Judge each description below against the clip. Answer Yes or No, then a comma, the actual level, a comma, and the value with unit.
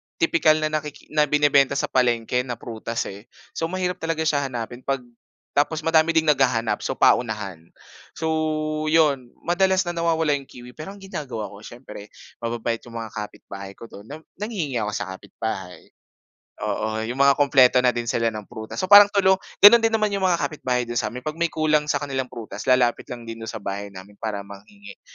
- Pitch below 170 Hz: Yes, low, 135 Hz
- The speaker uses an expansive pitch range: Yes, wide, 5.7 semitones